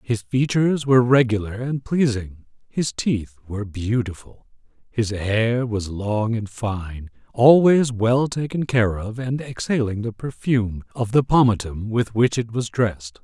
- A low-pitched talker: Yes, low, 115 Hz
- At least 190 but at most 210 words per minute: No, average, 150 wpm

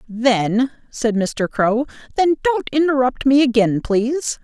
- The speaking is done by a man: No, female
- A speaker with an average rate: No, slow, 120 wpm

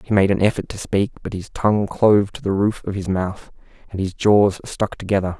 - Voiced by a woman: No, male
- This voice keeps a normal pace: No, fast, 235 wpm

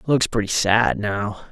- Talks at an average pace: Yes, average, 160 wpm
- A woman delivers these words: No, male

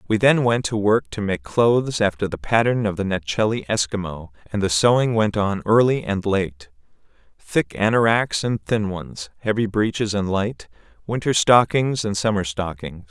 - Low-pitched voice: Yes, low, 105 Hz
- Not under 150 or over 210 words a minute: Yes, average, 170 wpm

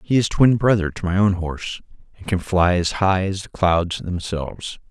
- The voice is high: No, very low, 95 Hz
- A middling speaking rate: No, fast, 210 wpm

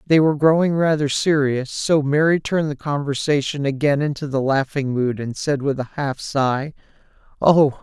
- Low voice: No, medium, 145 Hz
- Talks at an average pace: Yes, average, 170 wpm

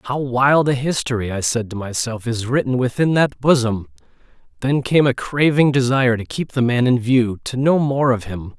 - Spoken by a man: Yes, male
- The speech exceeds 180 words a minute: Yes, average, 195 wpm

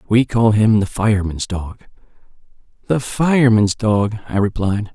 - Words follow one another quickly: No, slow, 135 wpm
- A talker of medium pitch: No, low, 110 Hz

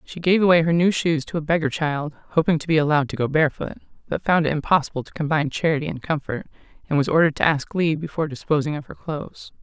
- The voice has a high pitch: No, medium, 155 Hz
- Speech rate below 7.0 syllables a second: No, 7.1 syllables/s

